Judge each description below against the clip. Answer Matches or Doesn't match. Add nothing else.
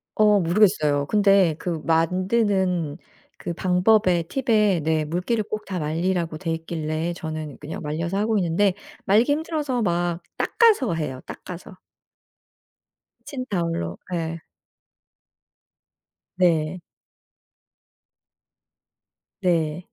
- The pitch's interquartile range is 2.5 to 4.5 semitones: Matches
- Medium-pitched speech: Matches